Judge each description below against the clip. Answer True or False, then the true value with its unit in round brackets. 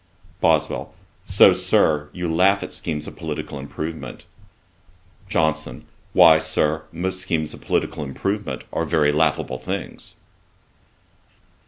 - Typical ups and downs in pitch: False (1.9 semitones)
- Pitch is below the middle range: True (80 Hz)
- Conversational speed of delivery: False (115 wpm)